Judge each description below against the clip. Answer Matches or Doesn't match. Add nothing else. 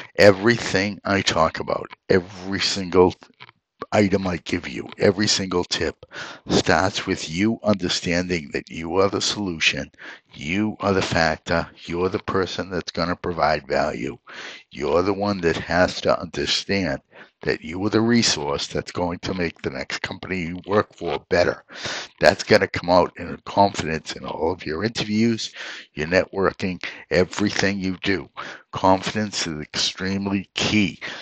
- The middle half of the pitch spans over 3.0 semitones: Doesn't match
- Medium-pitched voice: Doesn't match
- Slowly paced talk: Doesn't match